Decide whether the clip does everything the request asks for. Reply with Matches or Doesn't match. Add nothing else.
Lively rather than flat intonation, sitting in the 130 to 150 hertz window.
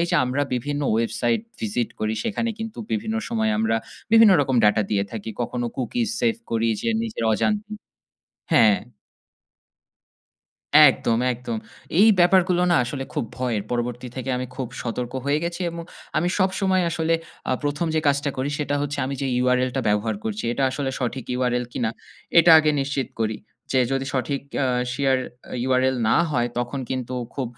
Matches